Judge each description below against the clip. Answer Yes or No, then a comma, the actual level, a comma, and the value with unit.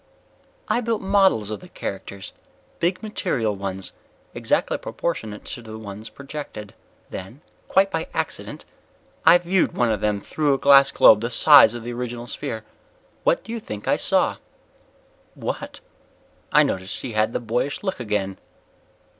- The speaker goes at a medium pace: Yes, average, 155 wpm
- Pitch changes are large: Yes, wide, 7.5 semitones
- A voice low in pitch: Yes, low, 120 Hz